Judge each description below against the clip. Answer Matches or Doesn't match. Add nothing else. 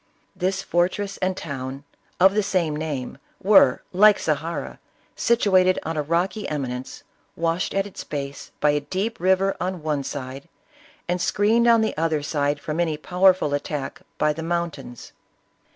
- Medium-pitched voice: Matches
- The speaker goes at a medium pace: Matches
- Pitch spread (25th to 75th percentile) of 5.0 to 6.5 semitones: Doesn't match